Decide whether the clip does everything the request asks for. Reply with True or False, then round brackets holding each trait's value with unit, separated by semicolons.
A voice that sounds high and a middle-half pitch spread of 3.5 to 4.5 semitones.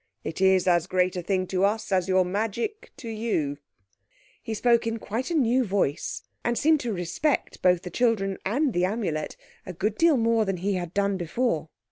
True (200 Hz; 4.2 semitones)